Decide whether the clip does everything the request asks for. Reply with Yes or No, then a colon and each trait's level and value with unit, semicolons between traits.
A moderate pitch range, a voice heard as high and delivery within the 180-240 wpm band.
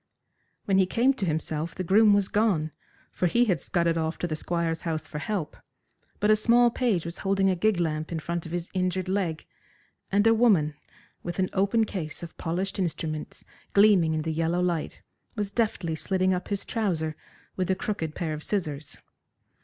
No: average, 3.8 semitones; medium, 180 Hz; average, 190 wpm